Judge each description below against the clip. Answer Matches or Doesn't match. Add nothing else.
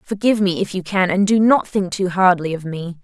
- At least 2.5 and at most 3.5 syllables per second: Doesn't match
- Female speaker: Matches